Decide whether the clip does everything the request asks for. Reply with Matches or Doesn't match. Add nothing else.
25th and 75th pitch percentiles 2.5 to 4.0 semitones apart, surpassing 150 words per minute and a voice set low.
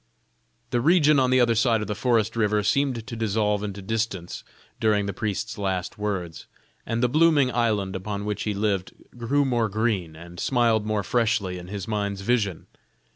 Matches